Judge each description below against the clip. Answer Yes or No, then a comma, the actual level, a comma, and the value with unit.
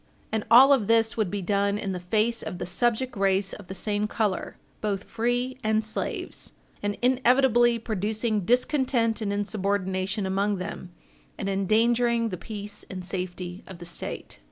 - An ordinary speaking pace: Yes, average, 160 wpm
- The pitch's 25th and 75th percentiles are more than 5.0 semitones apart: No, average, 3.2 semitones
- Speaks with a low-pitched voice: No, high, 210 Hz